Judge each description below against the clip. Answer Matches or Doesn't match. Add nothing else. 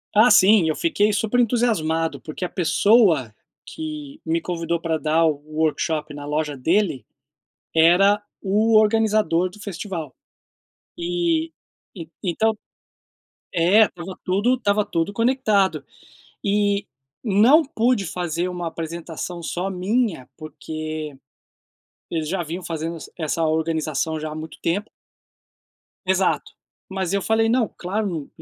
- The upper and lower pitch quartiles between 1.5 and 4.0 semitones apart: Doesn't match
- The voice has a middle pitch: Matches